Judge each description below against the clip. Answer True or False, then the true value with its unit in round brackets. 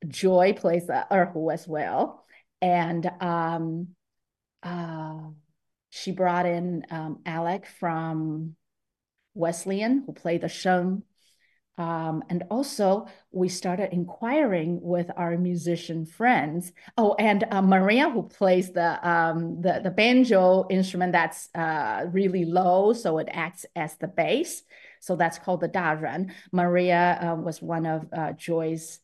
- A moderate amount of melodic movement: False (2.3 semitones)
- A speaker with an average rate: False (130 wpm)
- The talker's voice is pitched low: False (175 Hz)